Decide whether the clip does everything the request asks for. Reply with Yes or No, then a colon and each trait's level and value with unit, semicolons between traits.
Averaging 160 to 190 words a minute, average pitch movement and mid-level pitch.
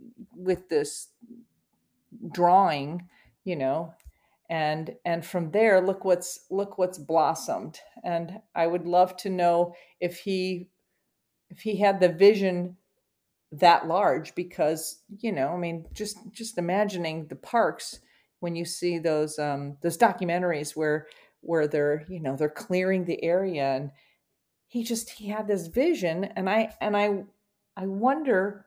No: average, 140 wpm; average, 3.6 semitones; medium, 180 Hz